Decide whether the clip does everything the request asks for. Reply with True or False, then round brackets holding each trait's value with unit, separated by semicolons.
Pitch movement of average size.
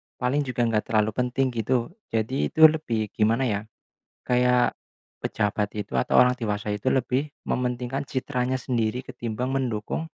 True (3.0 semitones)